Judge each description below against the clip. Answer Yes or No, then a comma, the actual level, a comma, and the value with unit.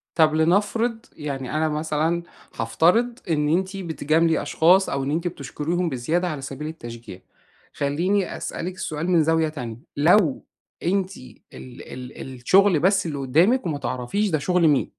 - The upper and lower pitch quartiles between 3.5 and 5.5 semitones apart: Yes, average, 4.3 semitones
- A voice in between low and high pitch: Yes, medium, 160 Hz